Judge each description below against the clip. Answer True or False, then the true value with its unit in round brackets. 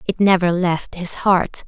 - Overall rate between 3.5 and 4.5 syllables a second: True (4.0 syllables/s)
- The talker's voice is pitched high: False (180 Hz)